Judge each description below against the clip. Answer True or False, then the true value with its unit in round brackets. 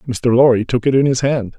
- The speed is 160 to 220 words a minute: False (265 wpm)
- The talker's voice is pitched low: True (125 Hz)